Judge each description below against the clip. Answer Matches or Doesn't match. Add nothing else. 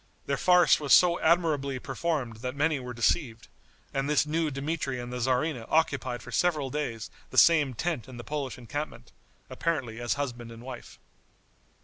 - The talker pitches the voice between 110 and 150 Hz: Matches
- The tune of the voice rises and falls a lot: Doesn't match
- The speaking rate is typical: Matches